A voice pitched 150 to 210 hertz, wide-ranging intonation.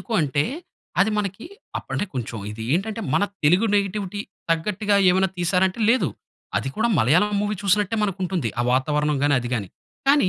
Yes: medium, 185 Hz; wide, 5.8 semitones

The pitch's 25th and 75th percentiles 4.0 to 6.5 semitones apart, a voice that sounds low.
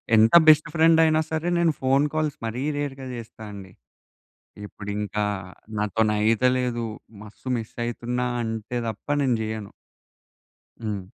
Yes: average, 4.4 semitones; low, 120 Hz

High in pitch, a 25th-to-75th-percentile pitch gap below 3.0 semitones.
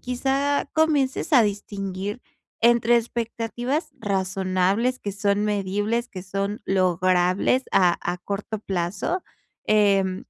No: high, 205 Hz; average, 3.9 semitones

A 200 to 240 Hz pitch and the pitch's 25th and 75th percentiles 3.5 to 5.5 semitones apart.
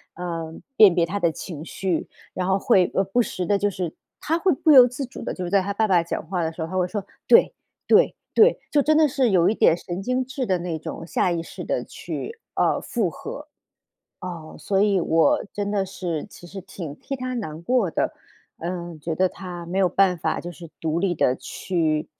No: medium, 185 Hz; average, 3.8 semitones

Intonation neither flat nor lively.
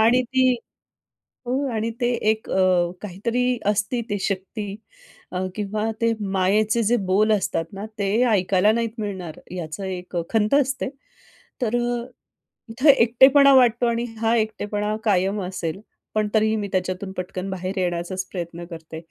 Yes: average, 3.7 semitones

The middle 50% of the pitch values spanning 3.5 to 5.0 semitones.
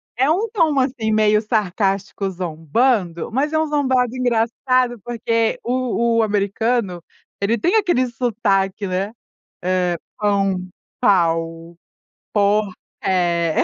Yes: average, 4.6 semitones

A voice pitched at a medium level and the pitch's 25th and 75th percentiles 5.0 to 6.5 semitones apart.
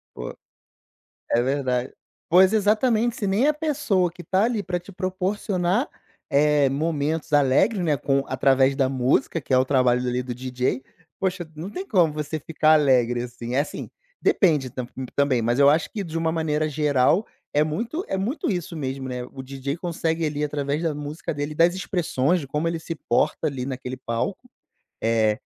Yes: medium, 150 Hz; wide, 5.4 semitones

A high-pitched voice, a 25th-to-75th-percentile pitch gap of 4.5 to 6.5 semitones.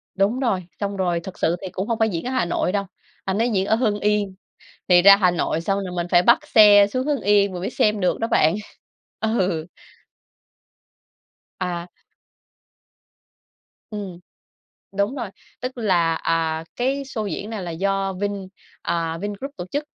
No: high, 195 Hz; average, 3.4 semitones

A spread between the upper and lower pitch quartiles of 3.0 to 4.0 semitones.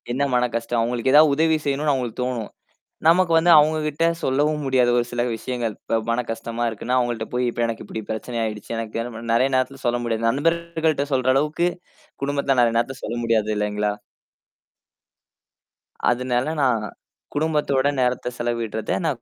Yes: average, 3.6 semitones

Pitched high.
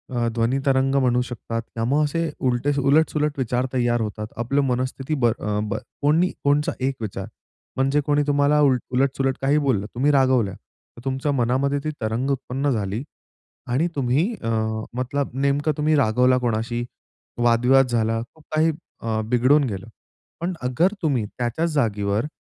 No: low, 130 Hz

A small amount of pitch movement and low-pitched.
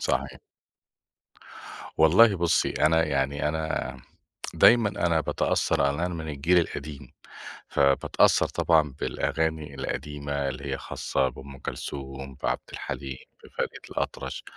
No: average, 3.0 semitones; very low, 75 Hz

